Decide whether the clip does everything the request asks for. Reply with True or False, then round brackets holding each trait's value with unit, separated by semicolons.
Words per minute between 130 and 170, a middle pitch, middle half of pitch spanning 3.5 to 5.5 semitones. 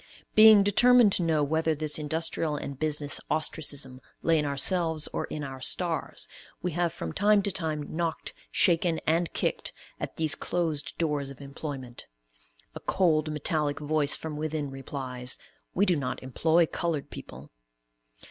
False (150 wpm; 155 Hz; 2.8 semitones)